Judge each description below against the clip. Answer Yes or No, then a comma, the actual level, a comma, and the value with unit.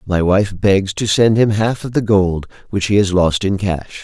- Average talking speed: No, fast, 240 wpm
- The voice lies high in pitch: No, low, 100 Hz